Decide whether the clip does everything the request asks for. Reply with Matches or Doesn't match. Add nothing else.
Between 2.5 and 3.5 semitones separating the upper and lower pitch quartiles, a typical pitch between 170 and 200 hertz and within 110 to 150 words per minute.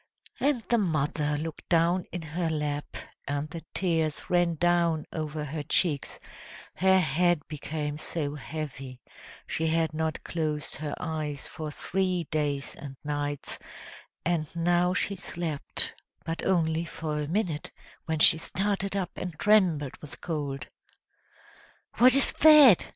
Doesn't match